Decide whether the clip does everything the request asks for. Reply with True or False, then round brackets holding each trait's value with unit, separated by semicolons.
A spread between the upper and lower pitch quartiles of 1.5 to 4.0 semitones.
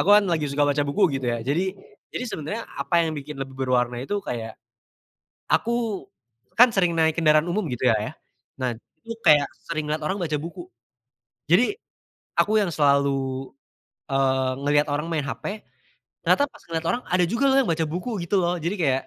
False (5.0 semitones)